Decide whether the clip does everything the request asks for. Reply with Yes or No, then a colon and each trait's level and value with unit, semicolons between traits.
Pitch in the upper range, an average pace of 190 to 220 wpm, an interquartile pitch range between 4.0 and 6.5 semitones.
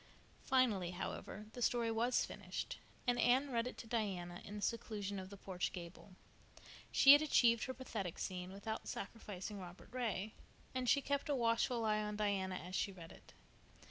No: high, 215 Hz; average, 175 wpm; average, 4.3 semitones